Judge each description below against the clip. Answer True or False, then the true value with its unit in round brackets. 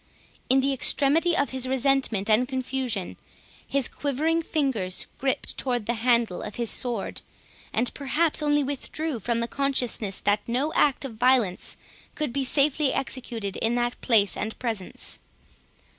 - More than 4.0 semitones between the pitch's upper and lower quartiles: False (3.3 semitones)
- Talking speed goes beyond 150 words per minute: False (145 wpm)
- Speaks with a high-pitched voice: True (255 Hz)